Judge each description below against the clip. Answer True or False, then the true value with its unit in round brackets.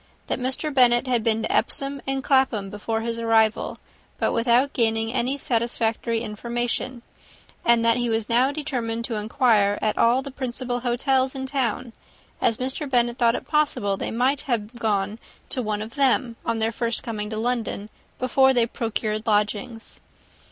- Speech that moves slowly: False (165 wpm)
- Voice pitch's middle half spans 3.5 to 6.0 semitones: False (2.5 semitones)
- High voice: True (235 Hz)